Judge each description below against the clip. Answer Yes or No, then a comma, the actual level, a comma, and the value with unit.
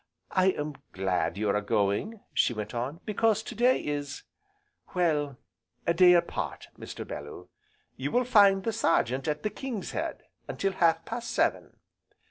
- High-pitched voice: No, medium, 165 Hz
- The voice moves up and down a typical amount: No, wide, 9.0 semitones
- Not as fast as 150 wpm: No, average, 155 wpm